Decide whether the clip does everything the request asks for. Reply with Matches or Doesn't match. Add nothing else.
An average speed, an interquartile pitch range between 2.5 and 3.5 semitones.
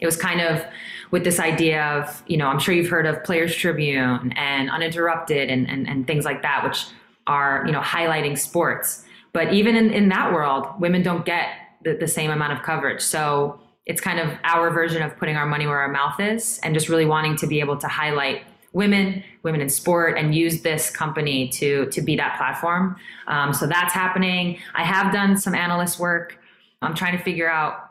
Doesn't match